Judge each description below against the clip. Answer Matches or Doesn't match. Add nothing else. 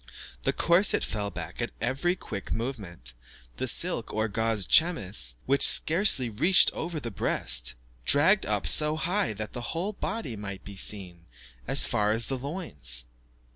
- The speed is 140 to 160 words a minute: Matches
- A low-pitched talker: Matches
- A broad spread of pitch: Matches